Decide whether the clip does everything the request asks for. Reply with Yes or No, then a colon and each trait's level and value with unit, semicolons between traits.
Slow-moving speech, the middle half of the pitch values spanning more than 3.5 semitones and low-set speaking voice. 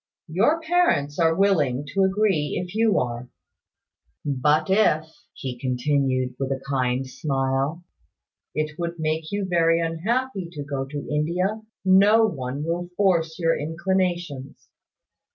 No: slow, 130 wpm; wide, 5.4 semitones; medium, 160 Hz